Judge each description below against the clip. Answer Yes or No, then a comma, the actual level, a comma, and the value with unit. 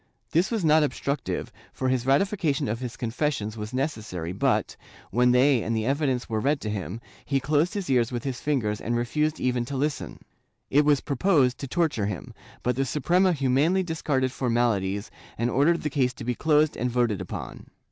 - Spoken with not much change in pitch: No, average, 4.1 semitones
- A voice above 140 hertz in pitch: No, low, 130 Hz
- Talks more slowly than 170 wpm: No, average, 190 wpm